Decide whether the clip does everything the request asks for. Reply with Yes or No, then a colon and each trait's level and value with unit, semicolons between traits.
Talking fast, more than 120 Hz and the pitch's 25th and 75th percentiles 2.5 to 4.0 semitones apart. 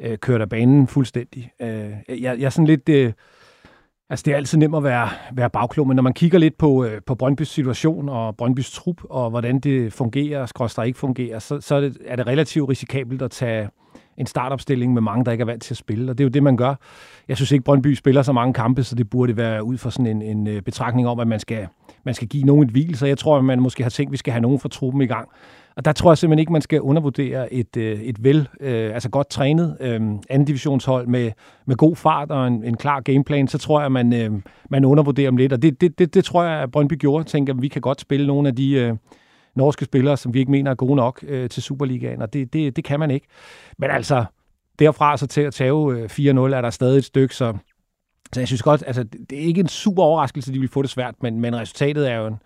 Yes: fast, 245 wpm; low, 135 Hz; average, 2.8 semitones